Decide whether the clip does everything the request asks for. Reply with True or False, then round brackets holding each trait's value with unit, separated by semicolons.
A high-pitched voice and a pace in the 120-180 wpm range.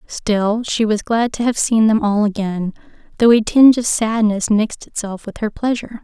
False (220 Hz; 200 wpm)